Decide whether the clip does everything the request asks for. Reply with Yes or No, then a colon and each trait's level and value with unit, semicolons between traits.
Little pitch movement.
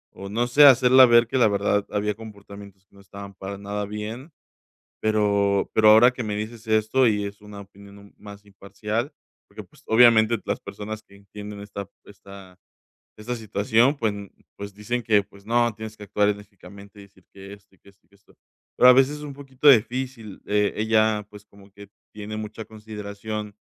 Yes: narrow, 1.9 semitones